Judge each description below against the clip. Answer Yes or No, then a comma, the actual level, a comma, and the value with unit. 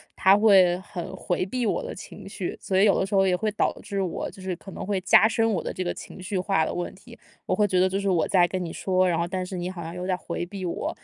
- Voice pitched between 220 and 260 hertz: No, medium, 185 Hz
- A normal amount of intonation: No, narrow, 1.8 semitones